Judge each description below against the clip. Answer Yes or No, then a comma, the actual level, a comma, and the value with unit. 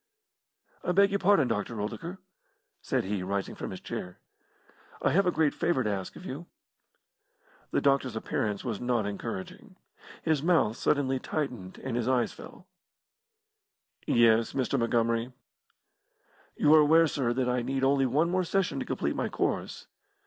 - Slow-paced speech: No, average, 155 wpm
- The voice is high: No, low, 130 Hz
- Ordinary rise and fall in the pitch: No, wide, 5.9 semitones